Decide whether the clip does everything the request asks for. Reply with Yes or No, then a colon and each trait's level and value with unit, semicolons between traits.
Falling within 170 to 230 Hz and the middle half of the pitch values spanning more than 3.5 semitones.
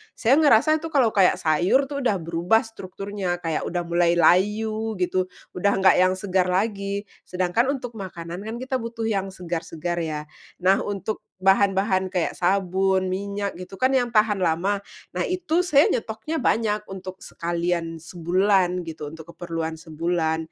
Yes: high, 190 Hz; average, 4.0 semitones